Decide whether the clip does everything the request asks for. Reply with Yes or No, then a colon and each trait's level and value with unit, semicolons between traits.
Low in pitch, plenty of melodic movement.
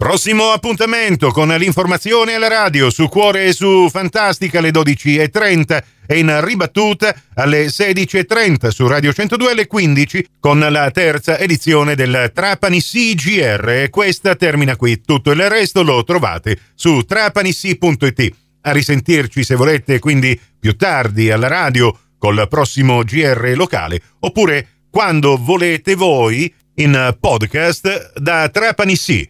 No: medium, 155 Hz; wide, 6.1 semitones